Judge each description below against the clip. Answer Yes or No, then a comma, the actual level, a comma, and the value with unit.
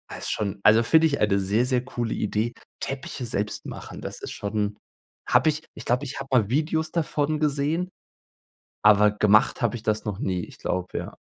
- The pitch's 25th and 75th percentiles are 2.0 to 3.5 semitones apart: No, average, 5.3 semitones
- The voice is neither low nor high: No, low, 120 Hz